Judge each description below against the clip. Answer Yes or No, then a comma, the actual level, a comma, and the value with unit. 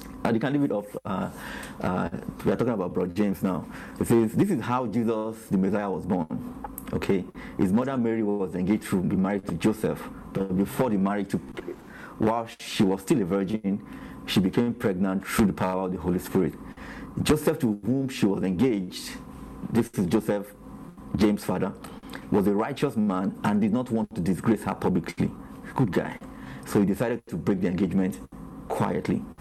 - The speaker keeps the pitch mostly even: No, average, 3.7 semitones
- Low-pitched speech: Yes, low, 110 Hz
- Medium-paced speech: Yes, average, 180 wpm